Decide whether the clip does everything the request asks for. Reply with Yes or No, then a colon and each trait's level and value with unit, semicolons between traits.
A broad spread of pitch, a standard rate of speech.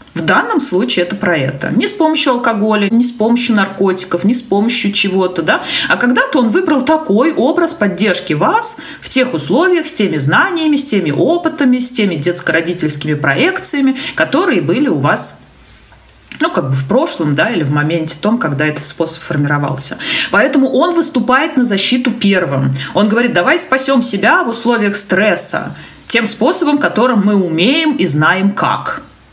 No: wide, 7.3 semitones; fast, 165 wpm